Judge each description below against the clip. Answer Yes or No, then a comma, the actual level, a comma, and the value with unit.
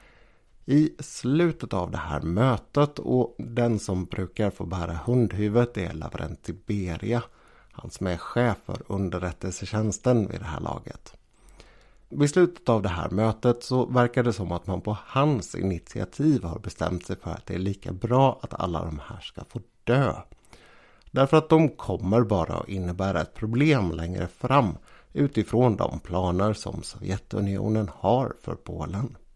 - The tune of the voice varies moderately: Yes, average, 5.0 semitones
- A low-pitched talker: Yes, low, 105 Hz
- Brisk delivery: No, average, 155 wpm